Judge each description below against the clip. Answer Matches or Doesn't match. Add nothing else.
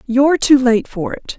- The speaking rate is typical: Doesn't match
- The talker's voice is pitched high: Matches